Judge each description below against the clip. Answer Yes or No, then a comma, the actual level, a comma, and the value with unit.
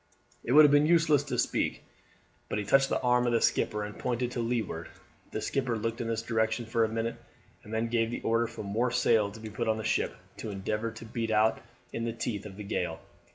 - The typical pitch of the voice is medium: No, low, 115 Hz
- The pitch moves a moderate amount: No, narrow, 1.8 semitones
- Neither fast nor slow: No, fast, 240 wpm